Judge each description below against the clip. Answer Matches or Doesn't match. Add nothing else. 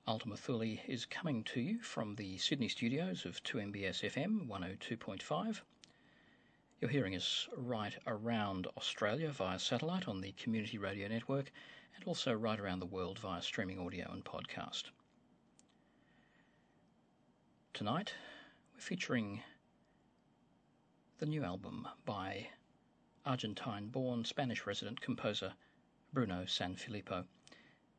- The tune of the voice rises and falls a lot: Doesn't match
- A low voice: Matches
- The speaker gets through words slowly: Matches